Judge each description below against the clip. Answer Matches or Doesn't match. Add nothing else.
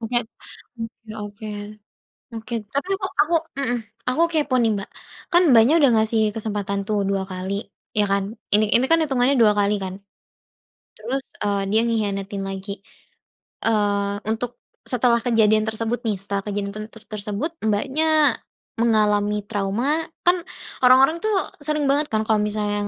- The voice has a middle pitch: Doesn't match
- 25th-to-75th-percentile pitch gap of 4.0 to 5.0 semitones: Doesn't match